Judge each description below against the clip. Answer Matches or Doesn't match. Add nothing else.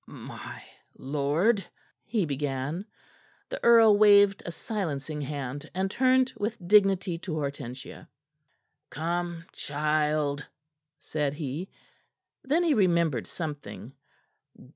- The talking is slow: Matches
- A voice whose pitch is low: Doesn't match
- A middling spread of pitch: Doesn't match